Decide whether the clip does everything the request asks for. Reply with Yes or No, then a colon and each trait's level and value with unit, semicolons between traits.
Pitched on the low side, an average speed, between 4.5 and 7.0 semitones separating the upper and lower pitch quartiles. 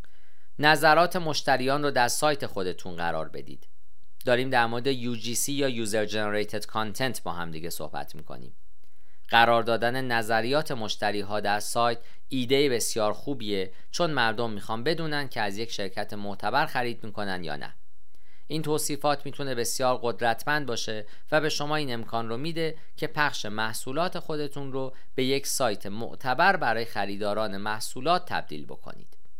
Yes: low, 120 Hz; average, 145 wpm; average, 5.2 semitones